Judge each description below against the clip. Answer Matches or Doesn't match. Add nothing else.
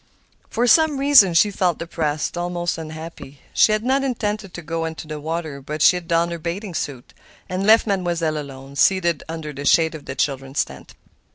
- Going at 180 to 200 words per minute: Matches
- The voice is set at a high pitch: Doesn't match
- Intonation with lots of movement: Doesn't match